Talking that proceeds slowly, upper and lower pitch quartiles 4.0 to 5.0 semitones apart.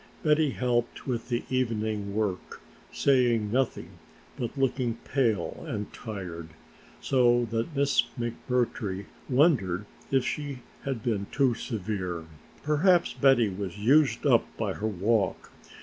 Yes: slow, 120 wpm; average, 4.4 semitones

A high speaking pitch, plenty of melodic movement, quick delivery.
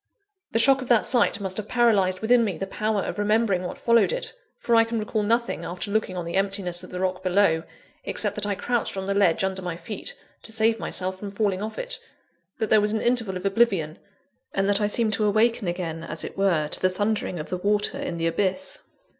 No: high, 200 Hz; average, 3.2 semitones; fast, 230 wpm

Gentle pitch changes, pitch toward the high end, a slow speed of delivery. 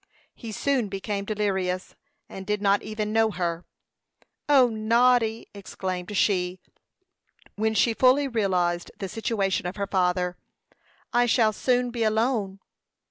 No: average, 3.2 semitones; high, 210 Hz; slow, 130 wpm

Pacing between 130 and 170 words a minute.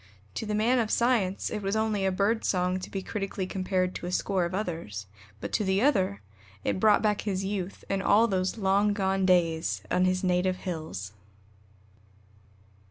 No: average, 180 wpm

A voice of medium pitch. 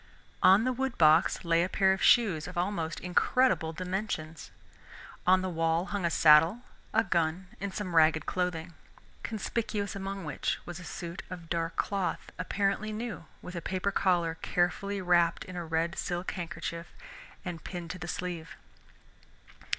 Yes: medium, 180 Hz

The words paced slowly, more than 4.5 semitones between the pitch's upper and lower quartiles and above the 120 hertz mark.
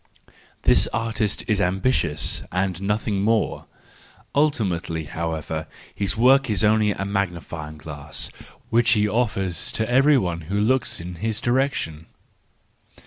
No: slow, 125 wpm; average, 5.2 semitones; low, 100 Hz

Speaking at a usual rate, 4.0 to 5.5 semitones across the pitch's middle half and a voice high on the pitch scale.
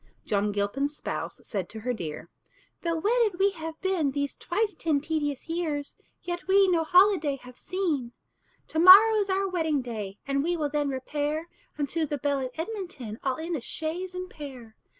Yes: average, 180 wpm; average, 4.9 semitones; very high, 310 Hz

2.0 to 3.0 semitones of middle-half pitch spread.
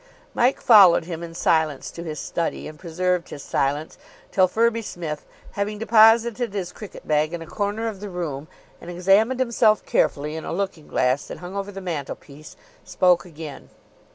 No: average, 4.7 semitones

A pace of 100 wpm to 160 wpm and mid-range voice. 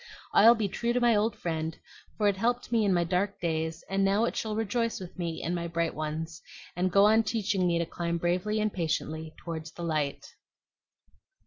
No: fast, 205 wpm; medium, 180 Hz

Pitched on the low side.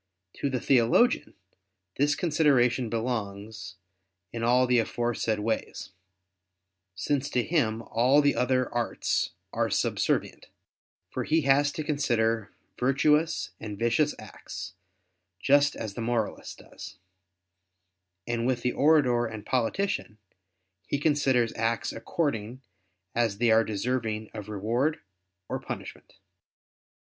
Yes: low, 120 Hz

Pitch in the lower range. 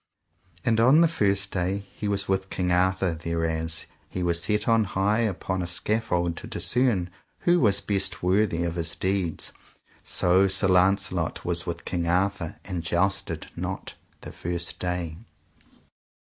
Yes: very low, 95 Hz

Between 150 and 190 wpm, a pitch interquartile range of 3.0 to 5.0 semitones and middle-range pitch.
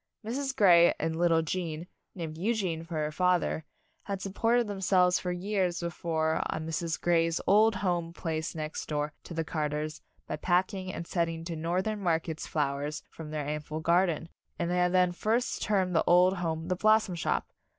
No: average, 175 wpm; narrow, 2.6 semitones; medium, 170 Hz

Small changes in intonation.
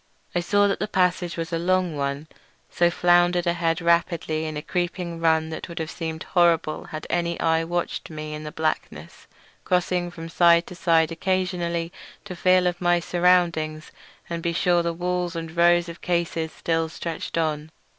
Yes: narrow, 1.4 semitones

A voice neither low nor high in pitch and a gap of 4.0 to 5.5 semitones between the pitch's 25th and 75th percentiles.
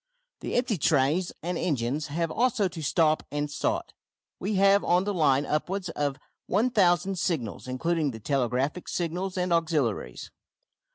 Yes: medium, 165 Hz; average, 4.4 semitones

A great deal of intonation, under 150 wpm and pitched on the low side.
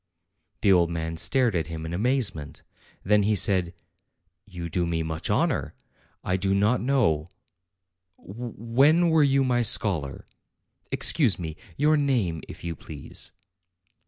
Yes: wide, 6.9 semitones; slow, 135 wpm; low, 100 Hz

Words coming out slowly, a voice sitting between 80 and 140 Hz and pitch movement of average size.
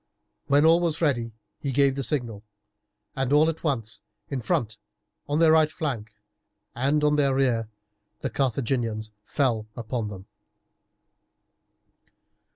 Yes: slow, 125 wpm; low, 135 Hz; average, 4.7 semitones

